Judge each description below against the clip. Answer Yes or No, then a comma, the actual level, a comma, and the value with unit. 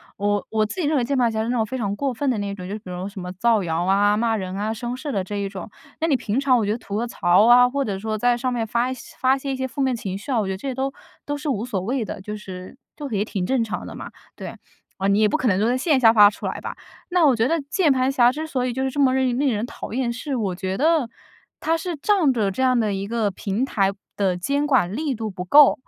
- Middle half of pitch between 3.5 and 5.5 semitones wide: Yes, average, 4.6 semitones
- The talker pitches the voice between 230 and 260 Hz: Yes, high, 235 Hz